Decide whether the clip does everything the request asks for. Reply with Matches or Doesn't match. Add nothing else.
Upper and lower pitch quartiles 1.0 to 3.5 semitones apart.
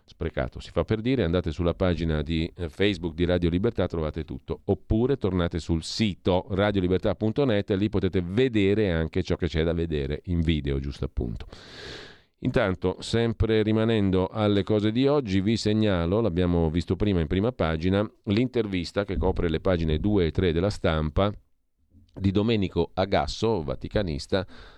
Doesn't match